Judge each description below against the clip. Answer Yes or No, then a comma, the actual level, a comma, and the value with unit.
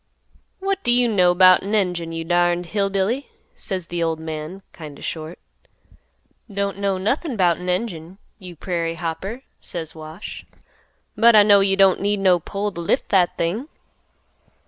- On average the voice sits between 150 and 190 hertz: Yes, medium, 185 Hz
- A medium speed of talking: Yes, average, 170 wpm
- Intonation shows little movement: No, average, 3.1 semitones